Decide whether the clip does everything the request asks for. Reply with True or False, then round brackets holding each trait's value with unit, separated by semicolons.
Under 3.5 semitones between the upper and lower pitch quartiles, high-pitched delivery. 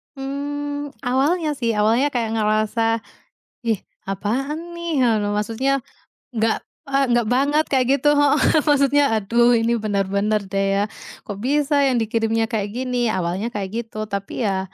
False (4.6 semitones; 235 Hz)